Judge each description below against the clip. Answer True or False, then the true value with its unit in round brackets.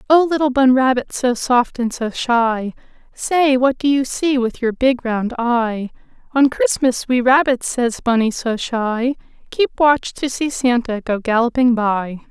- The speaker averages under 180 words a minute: True (170 wpm)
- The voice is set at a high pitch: True (250 Hz)